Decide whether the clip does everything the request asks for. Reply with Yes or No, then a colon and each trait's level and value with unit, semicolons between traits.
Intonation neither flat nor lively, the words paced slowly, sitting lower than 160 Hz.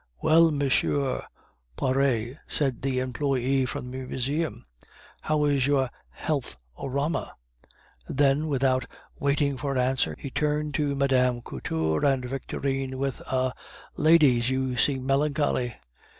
No: narrow, 1.9 semitones; slow, 130 wpm; low, 135 Hz